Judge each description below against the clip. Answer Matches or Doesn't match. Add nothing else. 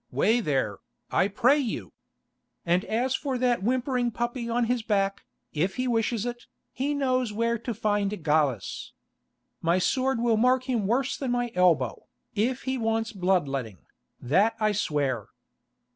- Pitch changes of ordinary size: Matches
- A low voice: Doesn't match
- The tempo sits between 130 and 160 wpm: Matches